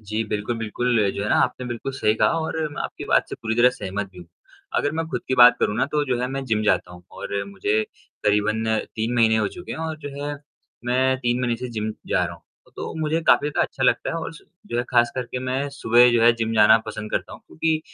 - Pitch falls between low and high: No, low, 120 Hz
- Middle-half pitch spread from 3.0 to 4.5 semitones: Yes, average, 3.5 semitones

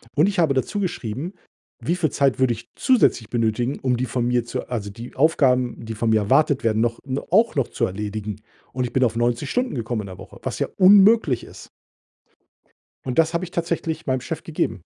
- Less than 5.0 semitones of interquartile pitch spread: No, wide, 5.8 semitones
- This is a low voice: Yes, low, 125 Hz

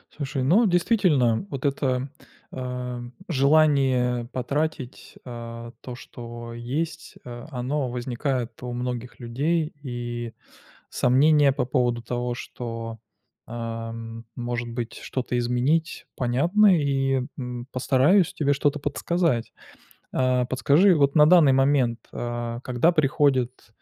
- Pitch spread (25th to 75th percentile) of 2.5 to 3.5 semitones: Yes, average, 3.2 semitones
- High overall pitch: No, low, 125 Hz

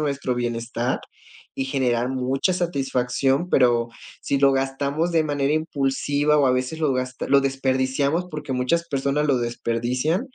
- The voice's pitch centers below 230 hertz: Yes, low, 135 Hz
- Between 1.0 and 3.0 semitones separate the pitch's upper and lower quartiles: Yes, narrow, 2.6 semitones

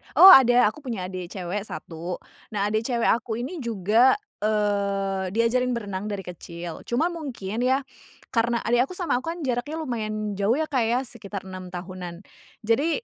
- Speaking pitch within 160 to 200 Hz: No, high, 220 Hz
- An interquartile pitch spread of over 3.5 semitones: Yes, average, 4.5 semitones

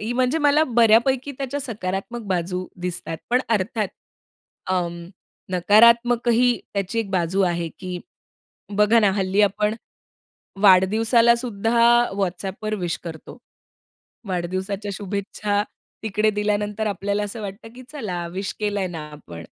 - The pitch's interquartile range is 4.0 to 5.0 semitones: No, average, 3.6 semitones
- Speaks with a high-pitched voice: Yes, high, 205 Hz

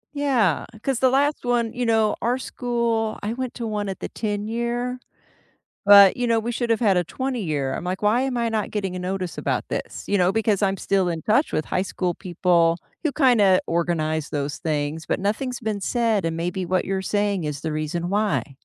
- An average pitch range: Yes, average, 5.0 semitones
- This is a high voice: Yes, high, 205 Hz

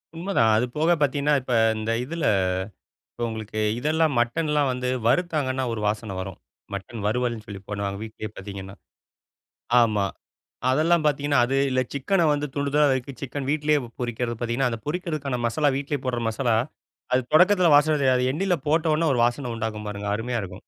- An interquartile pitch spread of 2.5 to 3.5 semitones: No, average, 4.8 semitones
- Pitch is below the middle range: Yes, low, 130 Hz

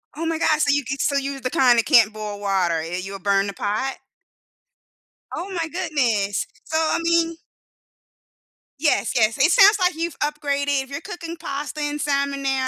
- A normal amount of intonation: No, wide, 6.4 semitones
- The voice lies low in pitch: No, very high, 280 Hz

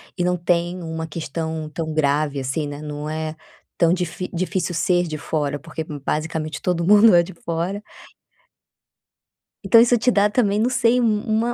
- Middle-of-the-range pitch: Yes, medium, 170 Hz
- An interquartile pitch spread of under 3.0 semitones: No, average, 4.3 semitones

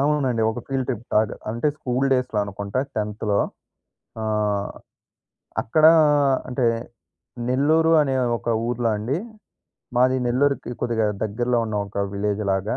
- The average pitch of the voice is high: No, low, 120 Hz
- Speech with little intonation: No, average, 3.7 semitones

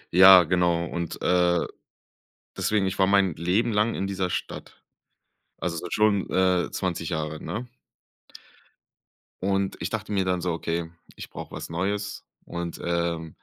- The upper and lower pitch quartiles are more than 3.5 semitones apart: No, narrow, 2.4 semitones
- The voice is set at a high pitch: No, very low, 90 Hz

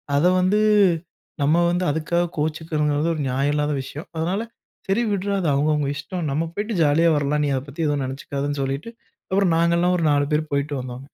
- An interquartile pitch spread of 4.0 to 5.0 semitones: No, average, 3.3 semitones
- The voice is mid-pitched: Yes, medium, 155 Hz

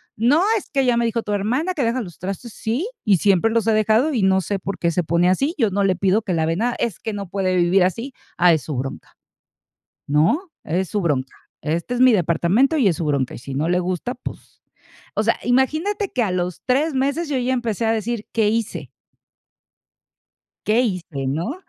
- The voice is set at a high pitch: Yes, high, 210 Hz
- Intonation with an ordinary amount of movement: No, wide, 5.7 semitones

